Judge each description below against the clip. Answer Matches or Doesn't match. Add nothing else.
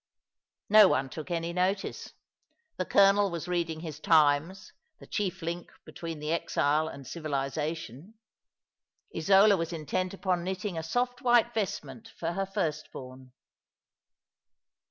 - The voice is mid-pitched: Matches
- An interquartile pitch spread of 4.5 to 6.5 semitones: Doesn't match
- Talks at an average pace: Doesn't match